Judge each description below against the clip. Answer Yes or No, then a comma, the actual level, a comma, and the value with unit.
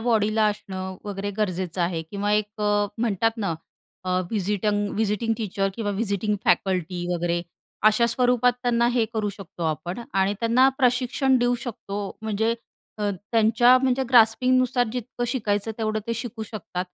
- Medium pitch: No, high, 215 Hz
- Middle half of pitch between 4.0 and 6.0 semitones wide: No, average, 3.2 semitones